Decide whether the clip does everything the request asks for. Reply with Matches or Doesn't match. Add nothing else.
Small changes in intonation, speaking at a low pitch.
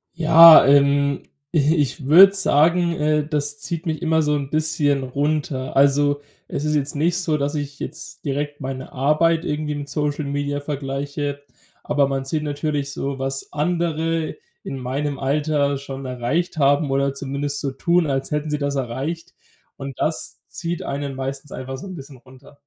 Doesn't match